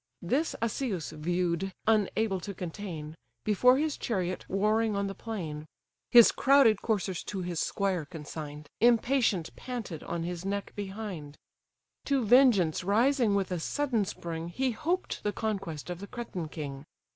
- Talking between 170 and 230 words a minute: No, average, 145 wpm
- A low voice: No, high, 200 Hz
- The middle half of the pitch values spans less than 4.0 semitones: No, average, 4.9 semitones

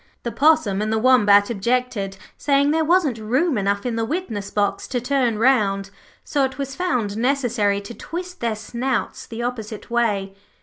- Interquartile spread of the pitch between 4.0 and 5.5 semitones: Yes, average, 4.6 semitones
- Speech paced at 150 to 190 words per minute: Yes, average, 170 wpm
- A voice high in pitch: Yes, high, 235 Hz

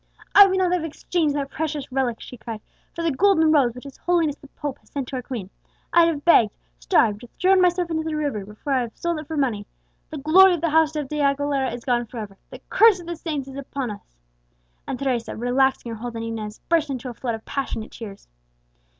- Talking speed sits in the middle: No, fast, 235 wpm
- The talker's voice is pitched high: Yes, very high, 275 Hz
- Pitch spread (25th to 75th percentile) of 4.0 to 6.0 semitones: Yes, average, 5.1 semitones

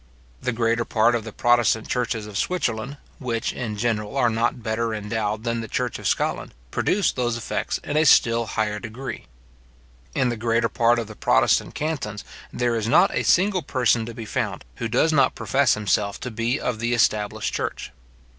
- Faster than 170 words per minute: Yes, average, 185 wpm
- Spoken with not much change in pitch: Yes, narrow, 2.2 semitones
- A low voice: Yes, low, 115 Hz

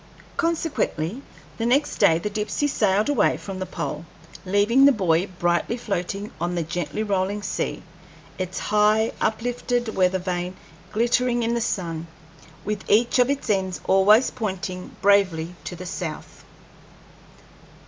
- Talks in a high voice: Yes, high, 200 Hz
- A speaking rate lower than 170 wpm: Yes, average, 140 wpm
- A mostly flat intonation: No, average, 4.3 semitones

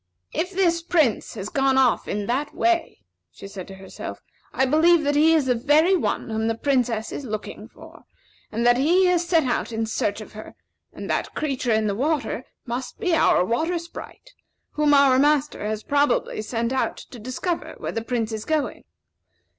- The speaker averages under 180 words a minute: No, average, 190 wpm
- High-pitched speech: Yes, very high, 265 Hz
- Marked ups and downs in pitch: Yes, wide, 5.8 semitones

